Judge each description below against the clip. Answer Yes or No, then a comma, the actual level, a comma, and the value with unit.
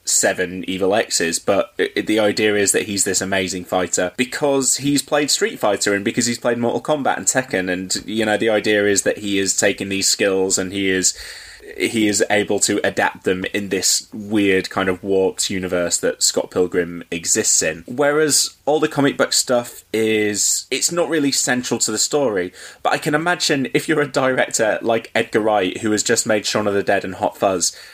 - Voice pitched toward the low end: Yes, low, 105 Hz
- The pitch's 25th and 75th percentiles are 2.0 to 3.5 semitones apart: No, average, 5.1 semitones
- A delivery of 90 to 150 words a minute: No, fast, 205 wpm